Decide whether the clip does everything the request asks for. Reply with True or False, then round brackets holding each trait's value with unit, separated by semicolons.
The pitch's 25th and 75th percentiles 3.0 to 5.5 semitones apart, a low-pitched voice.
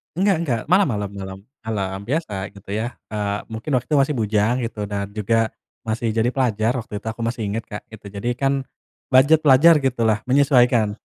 True (3.9 semitones; 115 Hz)